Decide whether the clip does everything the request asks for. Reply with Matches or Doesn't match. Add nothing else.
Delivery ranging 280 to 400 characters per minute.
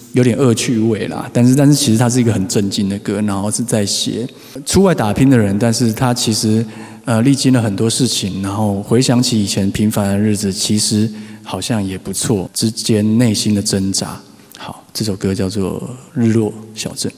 Matches